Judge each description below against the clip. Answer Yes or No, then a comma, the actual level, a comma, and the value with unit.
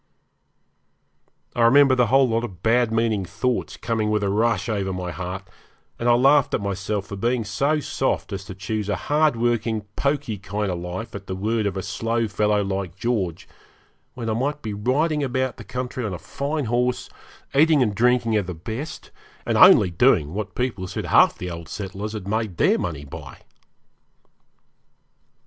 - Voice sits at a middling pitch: No, low, 110 Hz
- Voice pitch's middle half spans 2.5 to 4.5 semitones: Yes, average, 4.2 semitones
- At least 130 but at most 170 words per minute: No, average, 180 wpm